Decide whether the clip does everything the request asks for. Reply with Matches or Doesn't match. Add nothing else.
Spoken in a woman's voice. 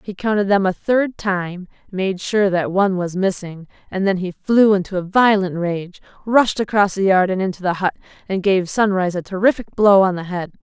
Matches